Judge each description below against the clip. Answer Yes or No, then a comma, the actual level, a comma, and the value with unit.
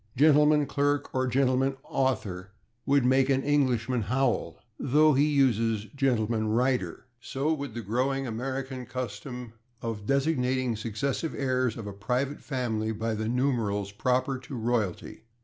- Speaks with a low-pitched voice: Yes, low, 125 Hz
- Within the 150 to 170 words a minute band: No, average, 140 wpm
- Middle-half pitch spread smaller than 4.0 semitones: Yes, average, 3.4 semitones